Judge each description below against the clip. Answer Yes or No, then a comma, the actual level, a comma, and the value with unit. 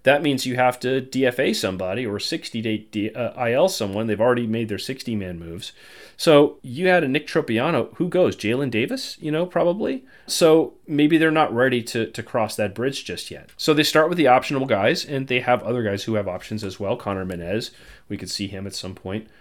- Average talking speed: No, fast, 225 wpm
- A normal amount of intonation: No, wide, 6.2 semitones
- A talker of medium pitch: No, low, 125 Hz